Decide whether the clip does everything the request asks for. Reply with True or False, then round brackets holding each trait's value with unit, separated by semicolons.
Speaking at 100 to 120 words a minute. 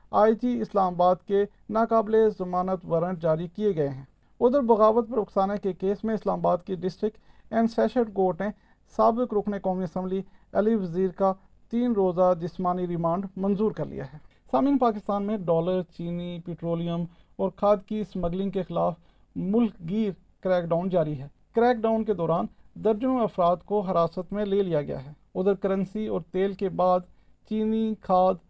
False (170 wpm)